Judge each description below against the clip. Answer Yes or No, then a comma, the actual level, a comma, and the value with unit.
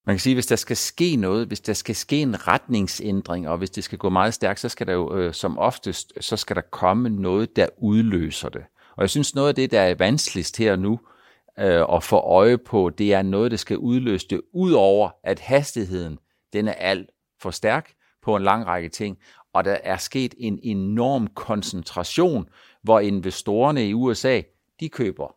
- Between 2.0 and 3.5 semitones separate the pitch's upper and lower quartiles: No, average, 4.1 semitones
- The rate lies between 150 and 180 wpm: No, average, 200 wpm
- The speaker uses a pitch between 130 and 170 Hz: No, low, 105 Hz